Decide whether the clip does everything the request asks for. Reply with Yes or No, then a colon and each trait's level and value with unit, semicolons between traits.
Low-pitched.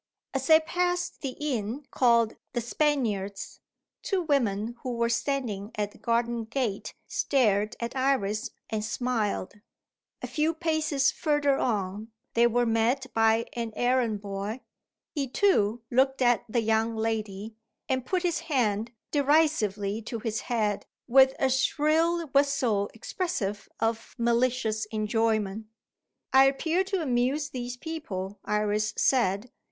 No: high, 235 Hz